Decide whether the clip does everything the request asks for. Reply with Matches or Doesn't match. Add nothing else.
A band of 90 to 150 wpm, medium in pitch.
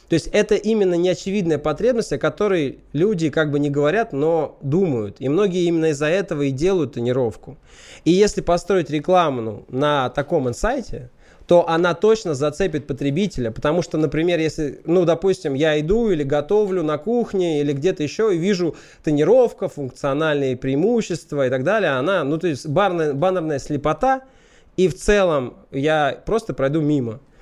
Doesn't match